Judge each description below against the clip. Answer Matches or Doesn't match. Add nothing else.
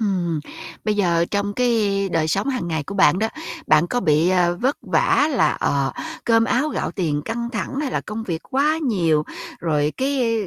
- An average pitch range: Doesn't match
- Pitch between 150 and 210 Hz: Matches